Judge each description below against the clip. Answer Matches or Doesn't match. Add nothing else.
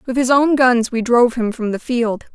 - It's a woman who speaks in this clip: Matches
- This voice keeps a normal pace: Doesn't match